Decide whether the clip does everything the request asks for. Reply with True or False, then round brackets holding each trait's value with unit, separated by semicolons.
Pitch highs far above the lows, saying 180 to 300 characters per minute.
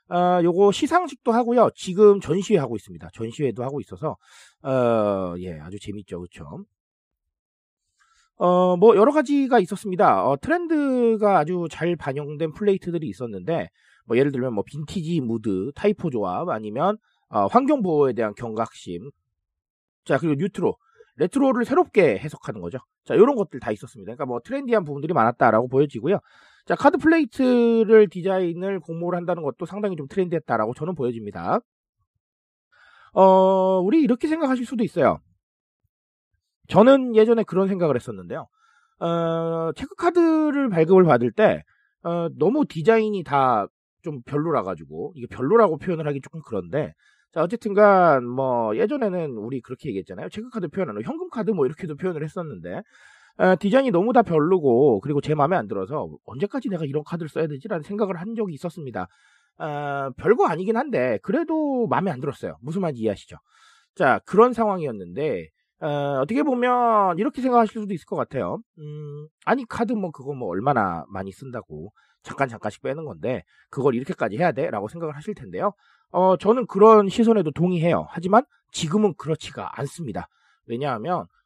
False (7.9 semitones; 370 characters per minute)